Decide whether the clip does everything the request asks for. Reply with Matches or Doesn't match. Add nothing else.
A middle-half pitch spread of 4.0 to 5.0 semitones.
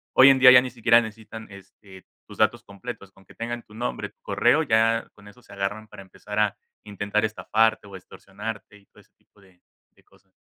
Doesn't match